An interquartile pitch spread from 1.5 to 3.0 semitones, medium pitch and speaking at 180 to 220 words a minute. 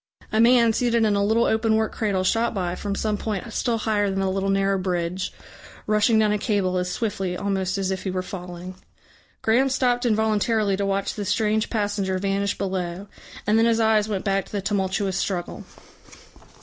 No: narrow, 2.5 semitones; high, 205 Hz; average, 190 wpm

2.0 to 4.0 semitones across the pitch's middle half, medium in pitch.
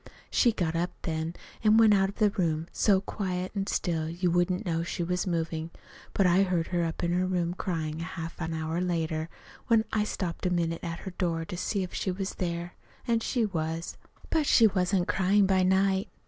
Yes: narrow, 2.6 semitones; medium, 180 Hz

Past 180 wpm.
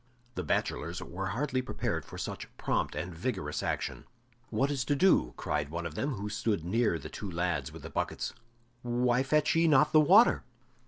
Yes: average, 190 wpm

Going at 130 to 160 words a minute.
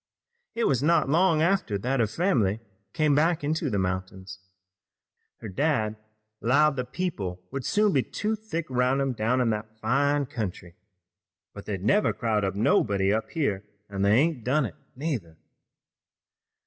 Yes: average, 155 wpm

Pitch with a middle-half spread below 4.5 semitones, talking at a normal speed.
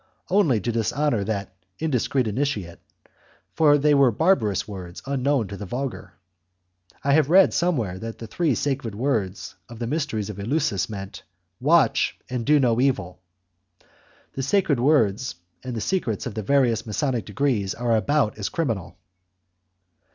No: wide, 5.4 semitones; average, 150 wpm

